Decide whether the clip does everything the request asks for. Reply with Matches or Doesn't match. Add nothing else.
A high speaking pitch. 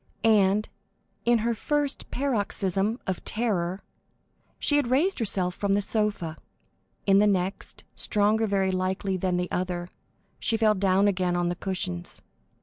Matches